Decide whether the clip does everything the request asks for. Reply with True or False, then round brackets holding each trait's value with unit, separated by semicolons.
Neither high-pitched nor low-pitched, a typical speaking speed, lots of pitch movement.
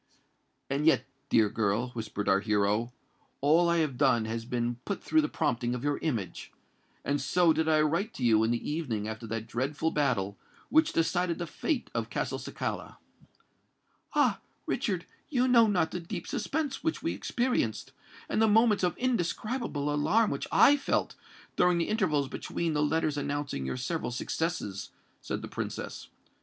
True (150 Hz; 165 wpm; 7.2 semitones)